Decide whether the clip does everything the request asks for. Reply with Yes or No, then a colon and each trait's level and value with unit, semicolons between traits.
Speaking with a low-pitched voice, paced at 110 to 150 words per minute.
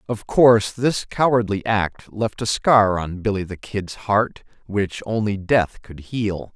No: low, 105 Hz; average, 165 wpm